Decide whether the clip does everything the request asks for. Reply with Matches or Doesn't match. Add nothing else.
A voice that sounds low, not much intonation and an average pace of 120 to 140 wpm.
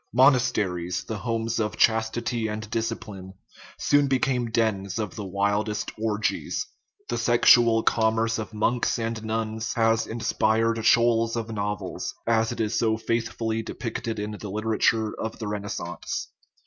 Matches